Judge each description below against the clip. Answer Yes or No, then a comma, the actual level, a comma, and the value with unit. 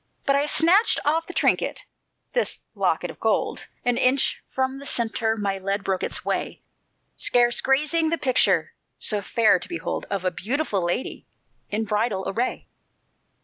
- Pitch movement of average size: No, wide, 5.8 semitones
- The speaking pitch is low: No, high, 240 Hz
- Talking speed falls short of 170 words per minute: Yes, average, 155 wpm